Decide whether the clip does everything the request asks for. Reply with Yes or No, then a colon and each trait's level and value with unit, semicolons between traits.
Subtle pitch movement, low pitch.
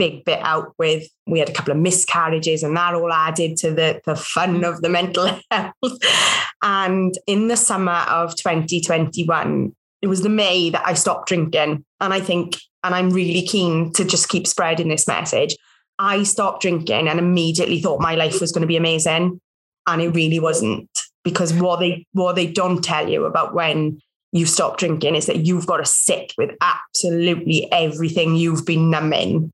No: narrow, 2.0 semitones; medium, 175 Hz